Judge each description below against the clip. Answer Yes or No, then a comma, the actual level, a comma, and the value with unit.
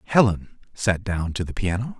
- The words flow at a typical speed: Yes, average, 180 wpm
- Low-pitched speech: Yes, very low, 95 Hz